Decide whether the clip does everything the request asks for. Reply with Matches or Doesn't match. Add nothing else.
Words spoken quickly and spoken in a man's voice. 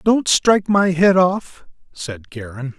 Doesn't match